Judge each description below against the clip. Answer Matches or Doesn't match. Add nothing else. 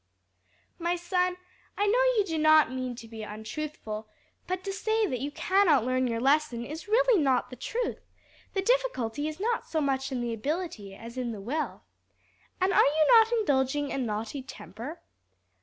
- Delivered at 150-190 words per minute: Matches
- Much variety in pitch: Matches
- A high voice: Matches